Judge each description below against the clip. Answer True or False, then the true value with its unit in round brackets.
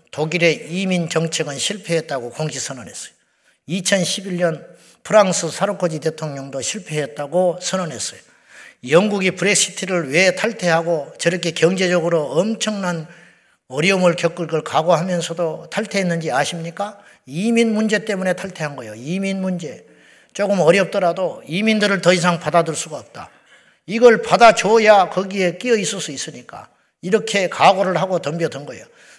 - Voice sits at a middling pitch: True (175 Hz)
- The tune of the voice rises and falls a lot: False (3.2 semitones)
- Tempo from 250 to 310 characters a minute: False (325 characters per minute)